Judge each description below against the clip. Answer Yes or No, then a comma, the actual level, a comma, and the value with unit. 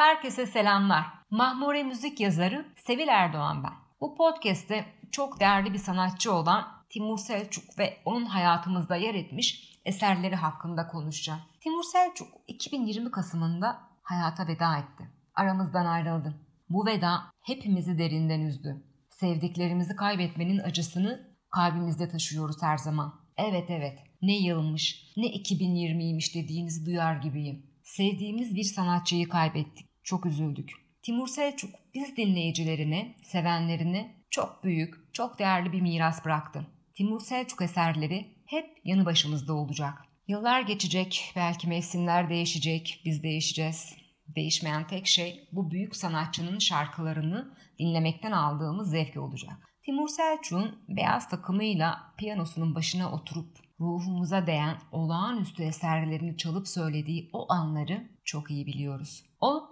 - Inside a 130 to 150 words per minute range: No, average, 120 wpm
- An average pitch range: Yes, average, 4.0 semitones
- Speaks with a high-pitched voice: No, medium, 175 Hz